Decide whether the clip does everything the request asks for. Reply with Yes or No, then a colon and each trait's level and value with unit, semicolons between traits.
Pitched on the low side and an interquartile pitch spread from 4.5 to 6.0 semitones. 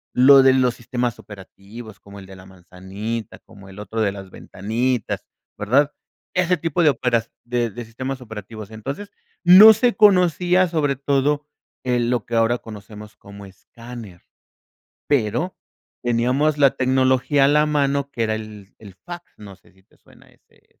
Yes: low, 120 Hz; average, 5.1 semitones